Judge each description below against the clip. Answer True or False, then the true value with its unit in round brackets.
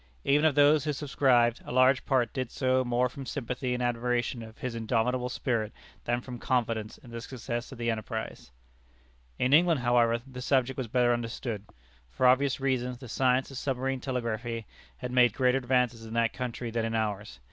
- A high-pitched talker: False (125 Hz)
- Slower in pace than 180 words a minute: False (185 wpm)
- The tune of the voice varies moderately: False (2.0 semitones)